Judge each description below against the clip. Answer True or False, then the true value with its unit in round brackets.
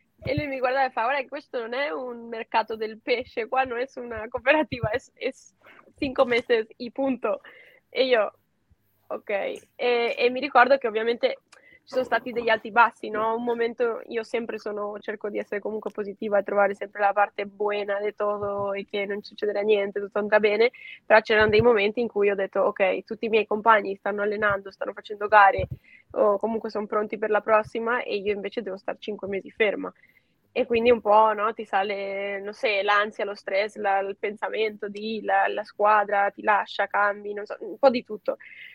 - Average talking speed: False (200 wpm)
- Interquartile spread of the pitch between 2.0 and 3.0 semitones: True (2.7 semitones)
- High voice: True (215 Hz)